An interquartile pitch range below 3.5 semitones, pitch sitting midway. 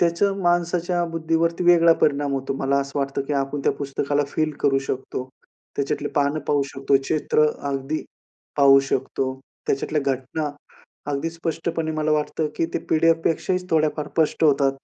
Yes: average, 3.0 semitones; medium, 150 Hz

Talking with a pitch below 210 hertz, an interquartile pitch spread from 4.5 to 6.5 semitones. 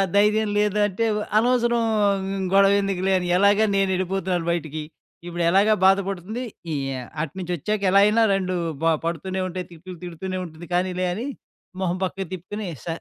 No: high, 190 Hz; narrow, 2.5 semitones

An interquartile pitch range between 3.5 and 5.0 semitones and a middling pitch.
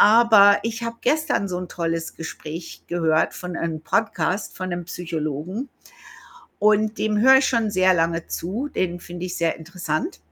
Yes: average, 4.4 semitones; medium, 180 Hz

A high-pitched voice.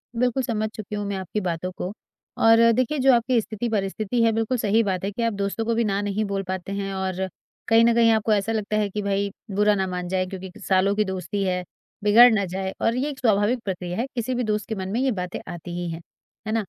Yes: high, 205 Hz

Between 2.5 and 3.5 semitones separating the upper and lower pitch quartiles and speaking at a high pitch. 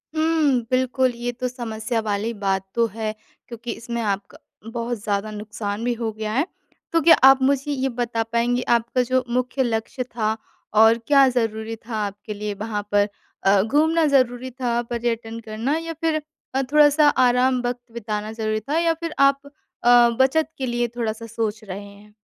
Yes: average, 3.2 semitones; high, 235 Hz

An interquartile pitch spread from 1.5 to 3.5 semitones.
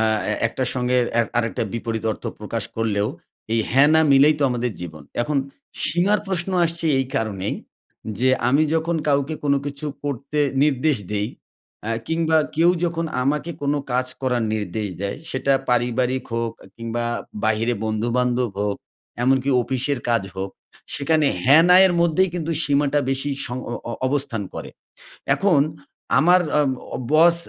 No: average, 4.8 semitones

